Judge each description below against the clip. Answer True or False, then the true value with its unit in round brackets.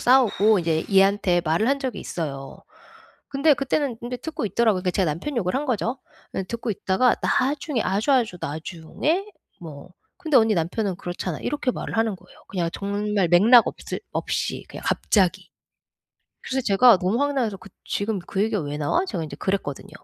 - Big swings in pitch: True (5.9 semitones)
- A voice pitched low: False (205 Hz)